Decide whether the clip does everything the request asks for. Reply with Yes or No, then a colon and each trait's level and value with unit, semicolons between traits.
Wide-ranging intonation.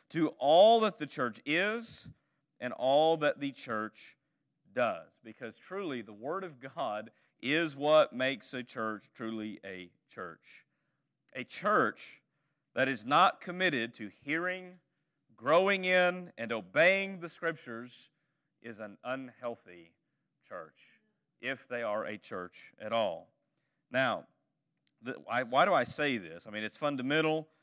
Yes: wide, 6.9 semitones